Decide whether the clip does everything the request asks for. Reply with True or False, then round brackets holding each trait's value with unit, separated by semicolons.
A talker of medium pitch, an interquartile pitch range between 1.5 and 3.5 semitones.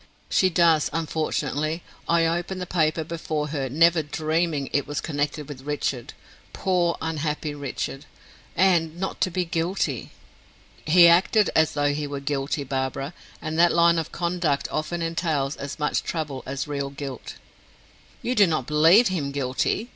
True (155 Hz; 2.9 semitones)